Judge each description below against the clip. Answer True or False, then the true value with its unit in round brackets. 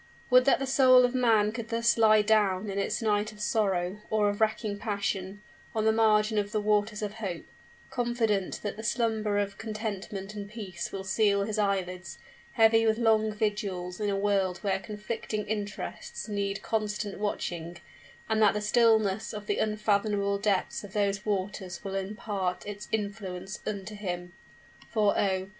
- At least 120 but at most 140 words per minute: False (165 wpm)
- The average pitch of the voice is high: True (210 Hz)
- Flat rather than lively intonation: True (1.7 semitones)